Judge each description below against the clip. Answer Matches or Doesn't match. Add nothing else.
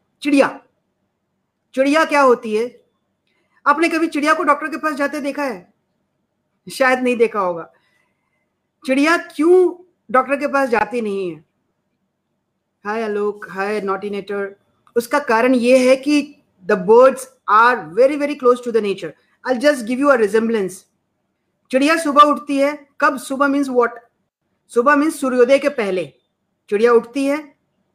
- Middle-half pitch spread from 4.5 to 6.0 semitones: Matches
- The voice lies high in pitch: Matches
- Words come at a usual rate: Matches